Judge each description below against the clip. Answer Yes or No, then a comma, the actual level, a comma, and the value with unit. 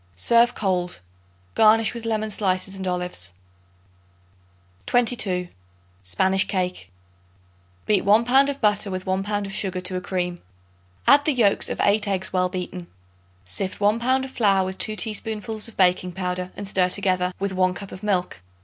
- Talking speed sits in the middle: Yes, average, 165 wpm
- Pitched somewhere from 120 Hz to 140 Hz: No, high, 195 Hz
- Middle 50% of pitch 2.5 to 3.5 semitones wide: Yes, average, 2.9 semitones